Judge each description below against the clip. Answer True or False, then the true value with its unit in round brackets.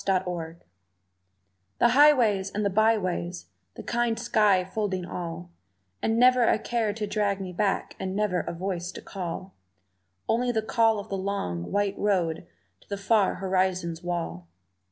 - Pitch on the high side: True (195 Hz)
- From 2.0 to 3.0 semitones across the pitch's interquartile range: False (3.4 semitones)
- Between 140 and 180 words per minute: True (155 wpm)